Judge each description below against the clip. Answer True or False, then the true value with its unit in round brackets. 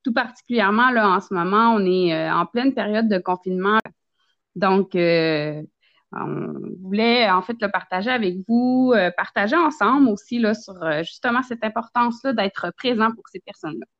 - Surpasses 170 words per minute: False (165 wpm)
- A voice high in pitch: True (210 Hz)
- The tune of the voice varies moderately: True (4.5 semitones)